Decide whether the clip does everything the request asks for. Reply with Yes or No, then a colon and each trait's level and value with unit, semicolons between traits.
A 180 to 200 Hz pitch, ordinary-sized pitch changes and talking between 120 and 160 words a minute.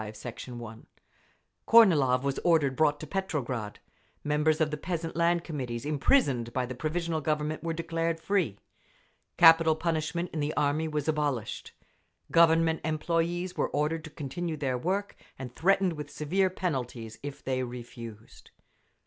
No: medium, 155 Hz; average, 4.1 semitones; average, 145 wpm